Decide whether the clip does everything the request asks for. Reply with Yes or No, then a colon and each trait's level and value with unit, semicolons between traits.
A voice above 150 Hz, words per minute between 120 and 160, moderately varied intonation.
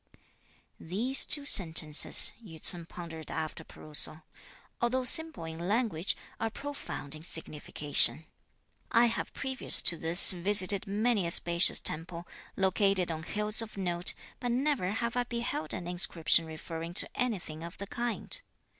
No: medium, 185 Hz; average, 140 wpm; wide, 6.2 semitones